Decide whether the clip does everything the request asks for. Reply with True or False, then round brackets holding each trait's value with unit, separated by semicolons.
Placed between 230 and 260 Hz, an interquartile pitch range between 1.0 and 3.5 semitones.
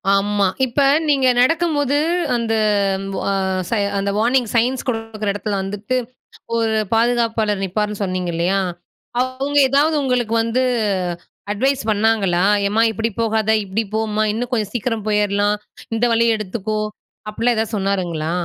False (220 Hz; 2.9 semitones)